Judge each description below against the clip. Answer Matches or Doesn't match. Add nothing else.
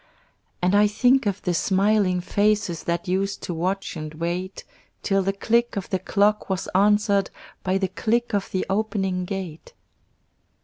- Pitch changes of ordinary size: Doesn't match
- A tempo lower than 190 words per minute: Matches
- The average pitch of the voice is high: Matches